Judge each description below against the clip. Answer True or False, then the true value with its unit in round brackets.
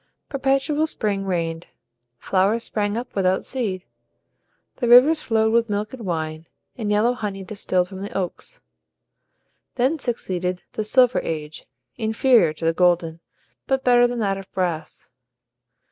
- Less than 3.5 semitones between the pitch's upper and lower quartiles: False (5.1 semitones)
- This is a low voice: False (205 Hz)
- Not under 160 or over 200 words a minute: False (140 wpm)